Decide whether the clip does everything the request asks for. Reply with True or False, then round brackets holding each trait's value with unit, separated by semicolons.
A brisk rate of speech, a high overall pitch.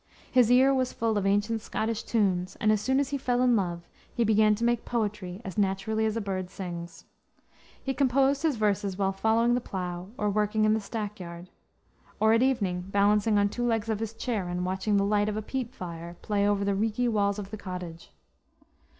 True (210 wpm; 210 Hz)